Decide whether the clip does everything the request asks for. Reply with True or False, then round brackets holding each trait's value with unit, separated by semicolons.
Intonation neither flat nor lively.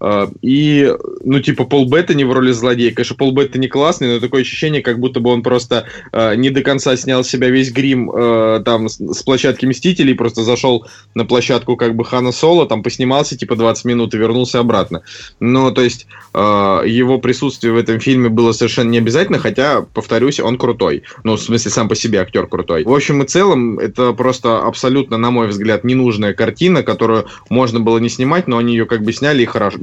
False (2.3 semitones)